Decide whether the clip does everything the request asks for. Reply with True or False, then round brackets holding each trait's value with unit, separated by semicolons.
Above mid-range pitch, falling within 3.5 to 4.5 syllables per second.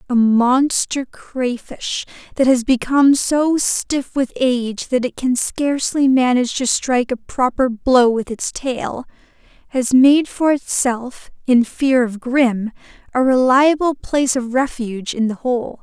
True (255 Hz; 4.0 syllables/s)